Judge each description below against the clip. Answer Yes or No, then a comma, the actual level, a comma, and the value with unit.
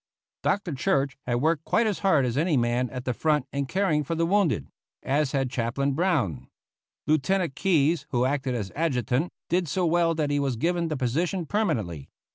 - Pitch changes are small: No, average, 4.9 semitones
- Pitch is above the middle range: No, medium, 145 Hz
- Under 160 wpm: No, average, 185 wpm